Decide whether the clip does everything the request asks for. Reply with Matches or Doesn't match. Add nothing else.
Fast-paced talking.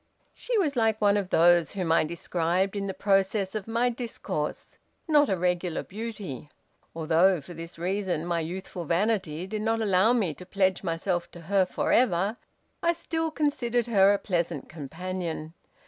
Doesn't match